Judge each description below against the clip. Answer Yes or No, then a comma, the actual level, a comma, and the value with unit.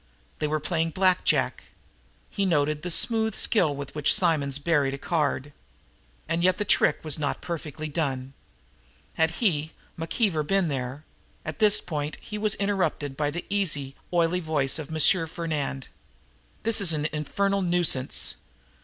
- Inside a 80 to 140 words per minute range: No, average, 155 wpm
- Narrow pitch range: No, average, 4.0 semitones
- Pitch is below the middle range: No, medium, 160 Hz